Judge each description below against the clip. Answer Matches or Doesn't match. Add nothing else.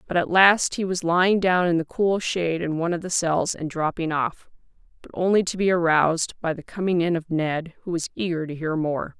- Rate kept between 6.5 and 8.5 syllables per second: Doesn't match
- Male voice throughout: Doesn't match